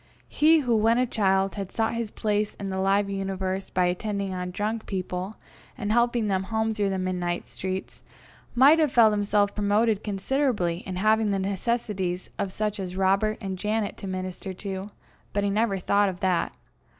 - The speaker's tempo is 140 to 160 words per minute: No, average, 180 wpm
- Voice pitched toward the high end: Yes, high, 200 Hz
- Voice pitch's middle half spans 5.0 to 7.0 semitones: No, narrow, 2.4 semitones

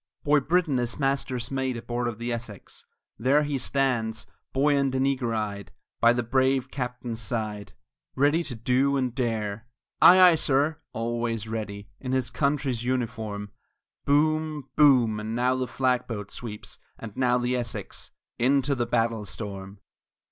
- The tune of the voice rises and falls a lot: No, average, 3.2 semitones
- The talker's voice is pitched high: No, low, 125 Hz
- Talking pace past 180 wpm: No, average, 155 wpm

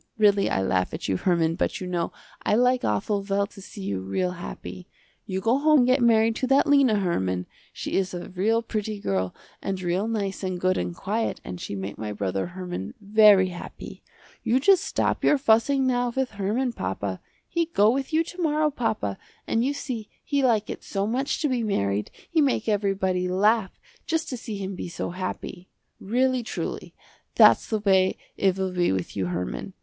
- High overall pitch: Yes, high, 200 Hz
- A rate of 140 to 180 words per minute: No, average, 195 wpm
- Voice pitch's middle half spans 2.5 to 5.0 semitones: No, wide, 5.5 semitones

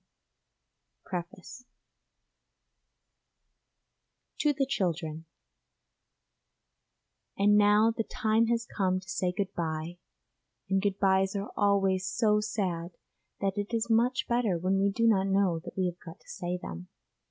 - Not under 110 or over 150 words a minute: Yes, slow, 135 wpm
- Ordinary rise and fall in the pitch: Yes, average, 3.1 semitones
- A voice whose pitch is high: Yes, high, 195 Hz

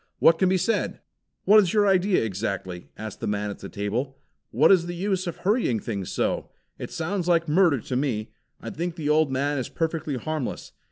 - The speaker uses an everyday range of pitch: No, wide, 8.0 semitones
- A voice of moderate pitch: Yes, medium, 155 Hz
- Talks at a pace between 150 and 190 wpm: No, fast, 205 wpm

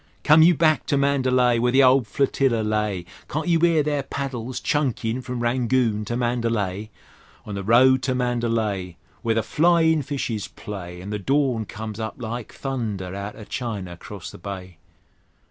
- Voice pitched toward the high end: No, low, 120 Hz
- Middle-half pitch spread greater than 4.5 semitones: No, average, 4.2 semitones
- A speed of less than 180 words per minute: Yes, average, 165 wpm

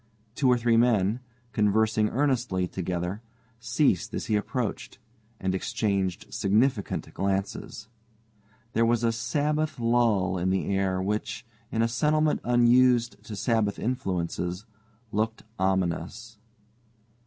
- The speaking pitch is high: No, low, 110 Hz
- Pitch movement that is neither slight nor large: Yes, average, 3.9 semitones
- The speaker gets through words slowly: Yes, slow, 115 wpm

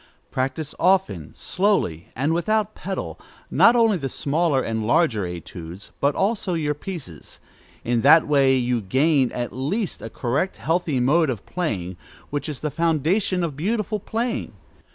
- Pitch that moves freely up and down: Yes, wide, 6.7 semitones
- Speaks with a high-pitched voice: No, medium, 150 Hz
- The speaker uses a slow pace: No, average, 150 wpm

